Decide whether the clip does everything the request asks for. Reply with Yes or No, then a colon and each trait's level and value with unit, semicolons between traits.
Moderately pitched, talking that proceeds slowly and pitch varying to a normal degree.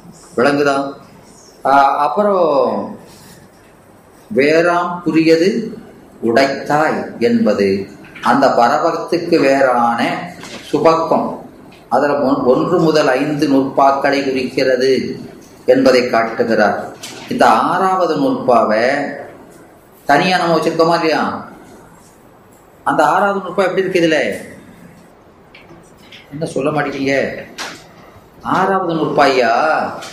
Yes: medium, 150 Hz; slow, 65 wpm; average, 4.3 semitones